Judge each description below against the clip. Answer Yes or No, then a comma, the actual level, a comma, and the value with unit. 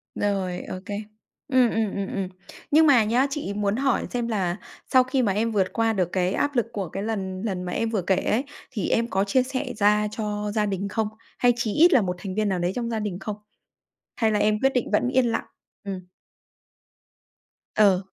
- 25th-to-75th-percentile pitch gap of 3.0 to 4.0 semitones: Yes, average, 3.4 semitones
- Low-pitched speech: No, high, 210 Hz